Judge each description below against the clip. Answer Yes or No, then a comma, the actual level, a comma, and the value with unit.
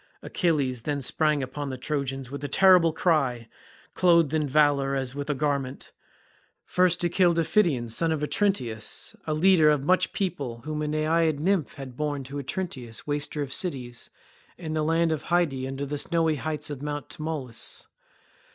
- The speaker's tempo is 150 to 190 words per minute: Yes, average, 170 wpm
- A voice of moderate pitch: Yes, medium, 150 Hz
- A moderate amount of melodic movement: Yes, average, 3.3 semitones